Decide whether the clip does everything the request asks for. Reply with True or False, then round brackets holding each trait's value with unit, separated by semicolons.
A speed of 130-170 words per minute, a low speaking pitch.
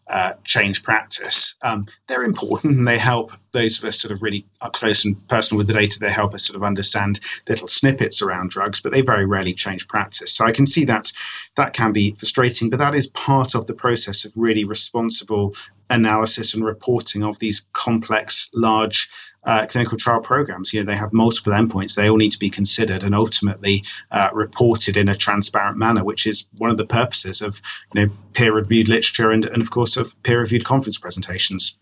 False (200 wpm; 110 Hz)